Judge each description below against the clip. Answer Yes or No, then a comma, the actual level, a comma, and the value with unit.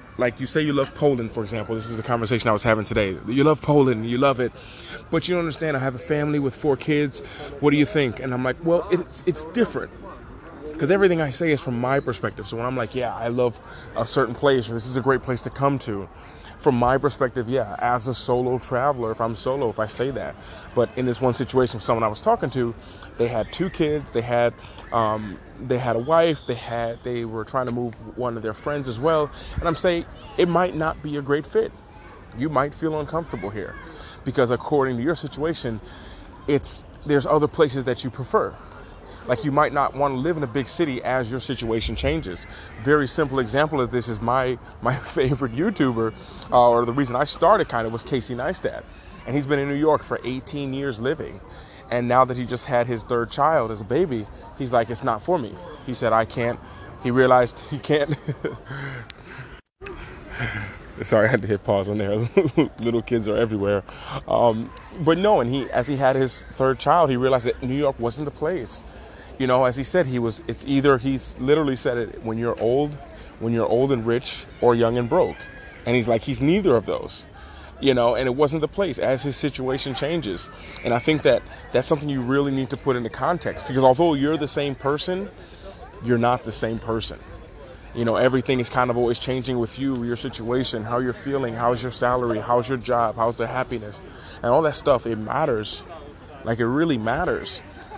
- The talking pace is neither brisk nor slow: No, fast, 215 wpm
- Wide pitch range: No, average, 3.6 semitones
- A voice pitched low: Yes, low, 125 Hz